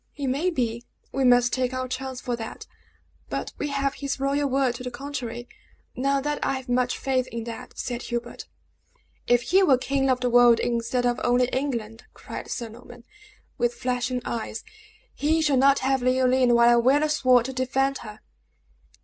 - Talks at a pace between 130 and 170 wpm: No, average, 185 wpm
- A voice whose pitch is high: Yes, very high, 255 Hz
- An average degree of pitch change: No, narrow, 2.0 semitones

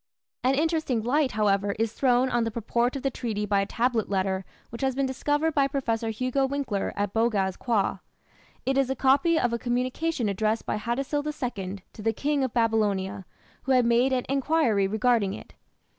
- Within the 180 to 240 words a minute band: Yes, average, 190 wpm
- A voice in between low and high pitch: No, high, 240 Hz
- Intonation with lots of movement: No, average, 4.1 semitones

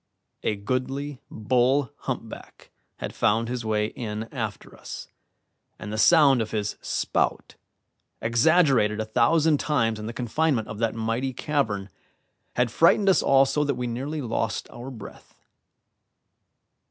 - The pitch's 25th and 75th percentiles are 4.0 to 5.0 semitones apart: Yes, average, 4.3 semitones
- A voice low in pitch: Yes, low, 120 Hz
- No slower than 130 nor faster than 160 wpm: Yes, average, 140 wpm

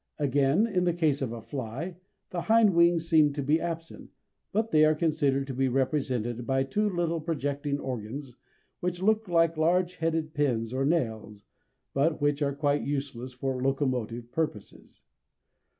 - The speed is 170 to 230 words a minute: No, average, 160 wpm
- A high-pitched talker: No, medium, 145 Hz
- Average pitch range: Yes, average, 4.0 semitones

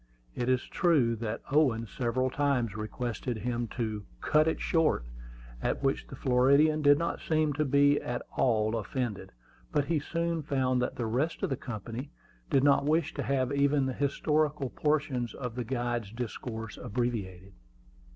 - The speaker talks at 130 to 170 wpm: Yes, average, 160 wpm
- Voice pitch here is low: Yes, low, 130 Hz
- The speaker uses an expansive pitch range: No, average, 3.6 semitones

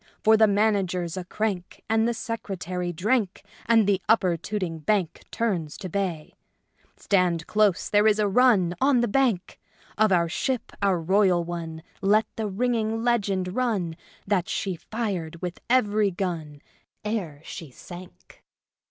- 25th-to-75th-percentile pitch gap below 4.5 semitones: Yes, average, 3.9 semitones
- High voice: Yes, high, 195 Hz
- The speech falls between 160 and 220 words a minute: No, average, 145 wpm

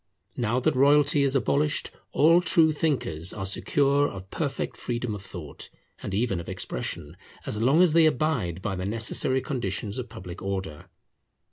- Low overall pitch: Yes, low, 125 Hz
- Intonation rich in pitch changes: Yes, wide, 7.0 semitones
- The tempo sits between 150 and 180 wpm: Yes, average, 160 wpm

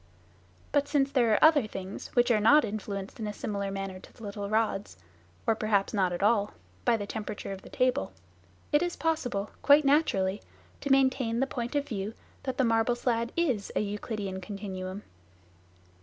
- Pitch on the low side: No, high, 220 Hz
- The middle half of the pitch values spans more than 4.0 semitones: Yes, average, 4.6 semitones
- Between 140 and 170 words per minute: No, average, 185 wpm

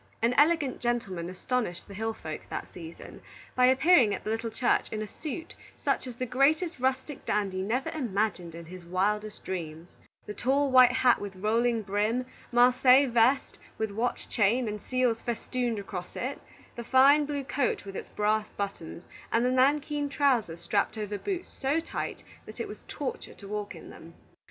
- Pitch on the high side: Yes, high, 235 Hz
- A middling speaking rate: Yes, average, 175 wpm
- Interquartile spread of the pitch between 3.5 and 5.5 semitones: Yes, average, 4.4 semitones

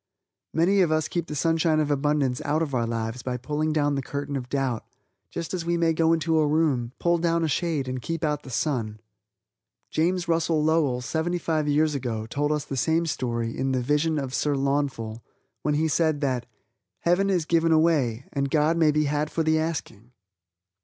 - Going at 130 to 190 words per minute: No, average, 200 wpm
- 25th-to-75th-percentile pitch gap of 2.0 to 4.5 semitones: Yes, average, 3.5 semitones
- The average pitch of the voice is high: No, medium, 150 Hz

